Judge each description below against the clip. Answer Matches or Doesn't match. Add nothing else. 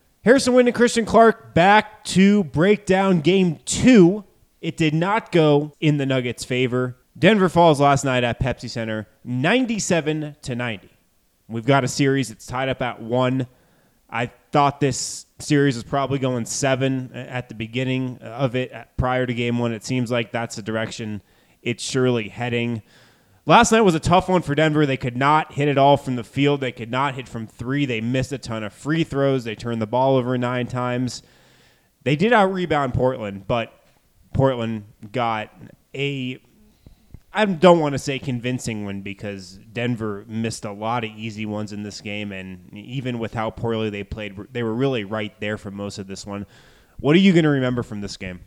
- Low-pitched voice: Matches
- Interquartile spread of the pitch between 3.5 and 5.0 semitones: Matches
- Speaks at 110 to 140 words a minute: Doesn't match